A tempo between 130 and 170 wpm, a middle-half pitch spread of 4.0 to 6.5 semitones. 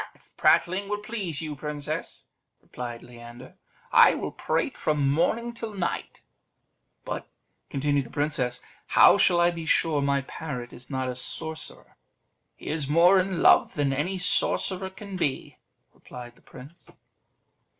Yes: average, 150 wpm; average, 5.0 semitones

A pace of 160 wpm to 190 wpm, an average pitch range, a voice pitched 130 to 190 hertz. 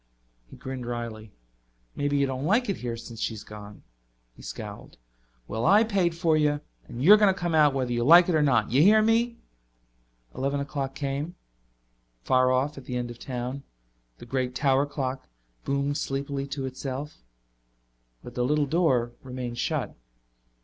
Yes: average, 165 wpm; average, 3.4 semitones; low, 135 Hz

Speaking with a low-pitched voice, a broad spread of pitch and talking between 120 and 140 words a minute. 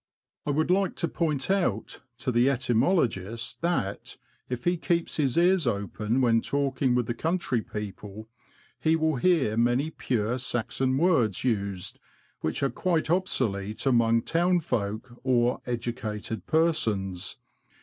Yes: low, 125 Hz; wide, 6.3 semitones; slow, 135 wpm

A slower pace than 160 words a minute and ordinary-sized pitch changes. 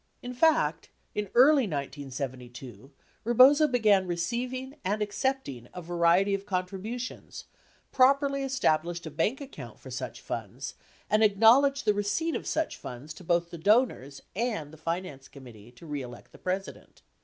No: average, 145 wpm; wide, 8.2 semitones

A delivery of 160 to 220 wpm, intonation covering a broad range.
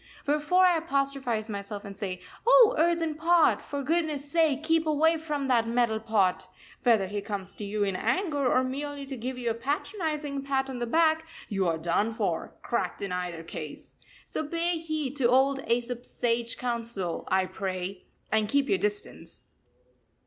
Yes: average, 170 wpm; wide, 6.5 semitones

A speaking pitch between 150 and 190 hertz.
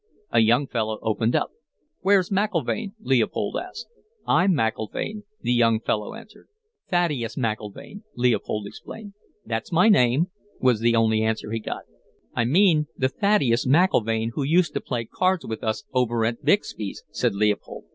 No: low, 120 Hz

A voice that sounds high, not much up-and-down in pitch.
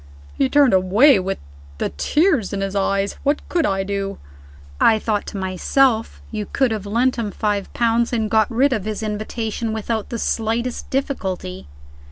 No: high, 220 Hz; average, 3.3 semitones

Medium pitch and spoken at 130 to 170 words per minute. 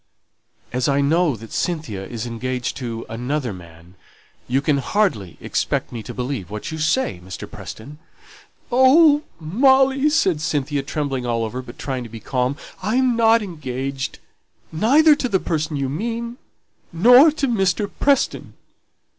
Yes: medium, 150 Hz; average, 150 wpm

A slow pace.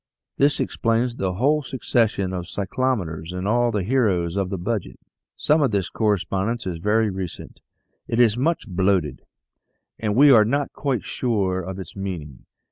No: average, 160 wpm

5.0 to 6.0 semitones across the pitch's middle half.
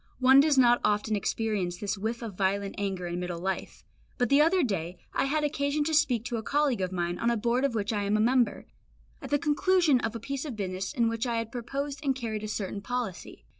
Yes: average, 5.3 semitones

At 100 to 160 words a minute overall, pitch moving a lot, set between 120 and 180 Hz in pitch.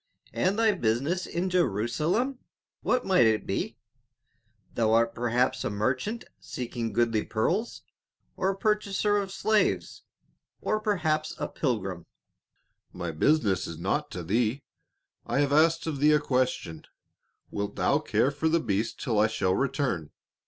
Yes: average, 145 wpm; wide, 8.5 semitones; low, 135 Hz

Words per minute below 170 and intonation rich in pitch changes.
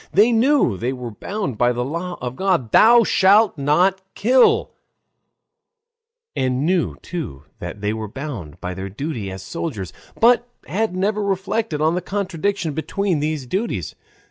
Yes: average, 150 wpm; wide, 8.4 semitones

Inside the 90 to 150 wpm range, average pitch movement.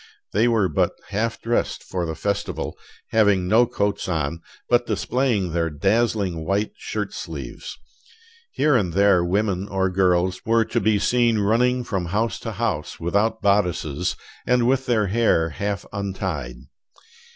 Yes: average, 145 wpm; average, 4.0 semitones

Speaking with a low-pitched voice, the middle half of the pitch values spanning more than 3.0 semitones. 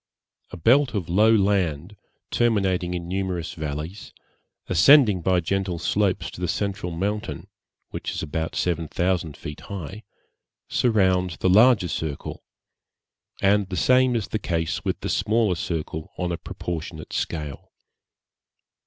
Yes: very low, 90 Hz; average, 3.7 semitones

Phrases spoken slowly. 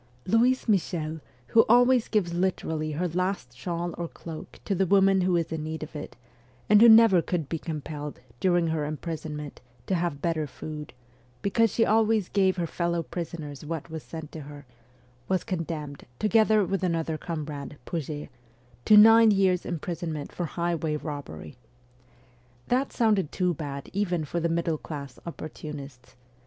No: average, 160 wpm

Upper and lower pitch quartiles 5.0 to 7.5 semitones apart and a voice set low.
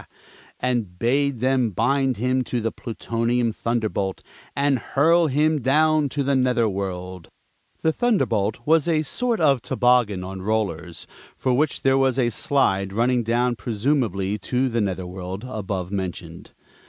Yes: average, 5.3 semitones; low, 120 Hz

